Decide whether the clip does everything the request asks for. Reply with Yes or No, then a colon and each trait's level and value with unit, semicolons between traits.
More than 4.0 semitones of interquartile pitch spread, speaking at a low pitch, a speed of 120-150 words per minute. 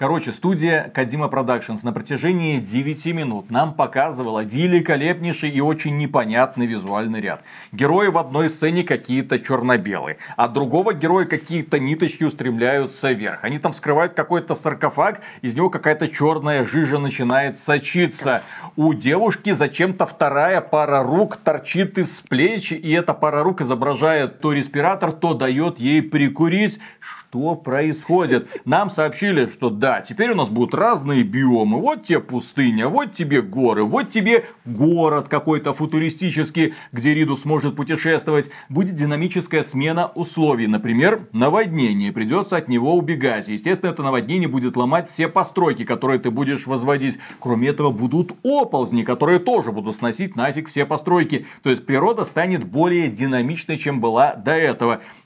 No: average, 4.5 semitones; medium, 155 Hz; average, 140 wpm